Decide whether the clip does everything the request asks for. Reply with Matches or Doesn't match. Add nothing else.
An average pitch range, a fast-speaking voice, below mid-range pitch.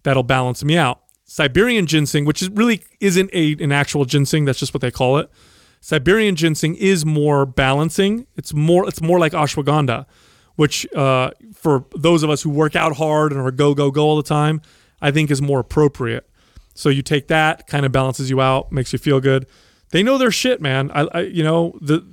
Doesn't match